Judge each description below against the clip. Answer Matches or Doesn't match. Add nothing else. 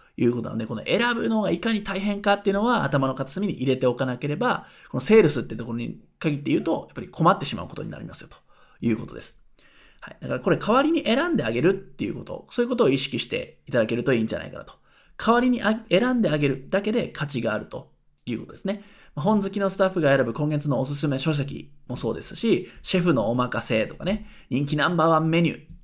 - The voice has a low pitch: Doesn't match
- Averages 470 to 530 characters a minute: Matches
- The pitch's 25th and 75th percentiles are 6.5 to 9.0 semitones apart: Matches